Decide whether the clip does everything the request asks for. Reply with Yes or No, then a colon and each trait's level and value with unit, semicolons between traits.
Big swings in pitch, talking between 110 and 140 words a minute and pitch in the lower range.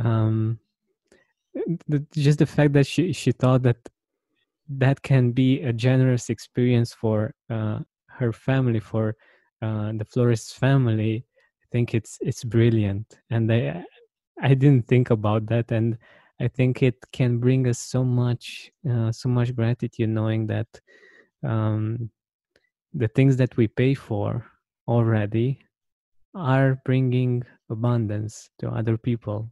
No: average, 2.7 semitones; slow, 135 wpm; low, 120 Hz